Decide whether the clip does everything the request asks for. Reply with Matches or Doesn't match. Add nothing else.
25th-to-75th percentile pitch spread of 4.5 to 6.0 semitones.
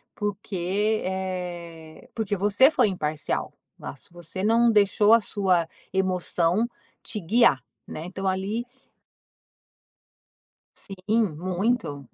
Doesn't match